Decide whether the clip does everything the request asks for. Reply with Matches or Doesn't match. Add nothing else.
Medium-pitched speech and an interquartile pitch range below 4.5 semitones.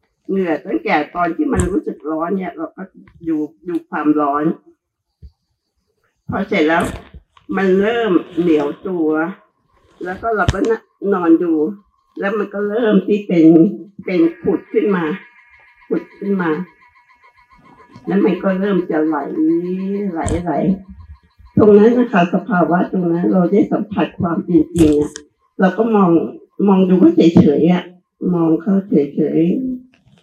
Matches